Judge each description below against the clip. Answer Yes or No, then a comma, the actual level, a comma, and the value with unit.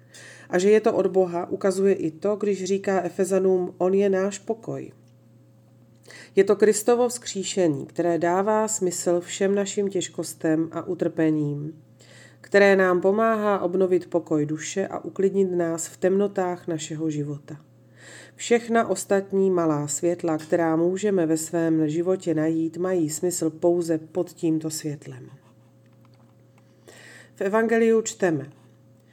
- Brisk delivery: No, average, 125 wpm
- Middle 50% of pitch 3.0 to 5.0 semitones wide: Yes, average, 3.4 semitones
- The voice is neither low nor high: Yes, medium, 175 Hz